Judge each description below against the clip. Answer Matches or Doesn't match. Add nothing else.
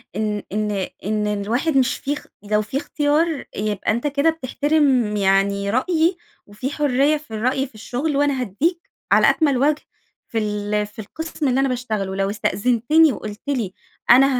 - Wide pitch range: Matches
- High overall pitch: Matches